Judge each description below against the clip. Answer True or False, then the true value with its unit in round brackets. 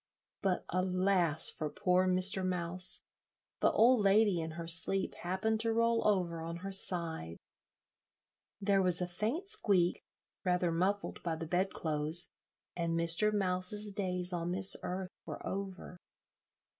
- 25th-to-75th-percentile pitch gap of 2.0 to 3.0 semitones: True (2.5 semitones)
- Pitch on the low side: False (185 Hz)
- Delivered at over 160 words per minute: False (135 wpm)